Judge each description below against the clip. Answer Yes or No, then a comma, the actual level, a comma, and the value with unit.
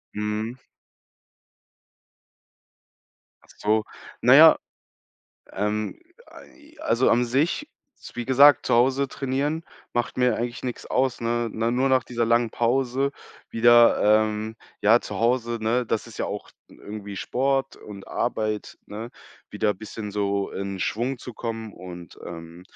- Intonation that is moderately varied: Yes, average, 3.2 semitones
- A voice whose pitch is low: Yes, low, 115 Hz